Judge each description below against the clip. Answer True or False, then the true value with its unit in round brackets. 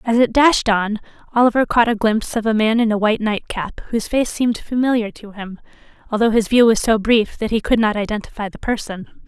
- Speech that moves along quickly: True (220 wpm)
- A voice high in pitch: True (220 Hz)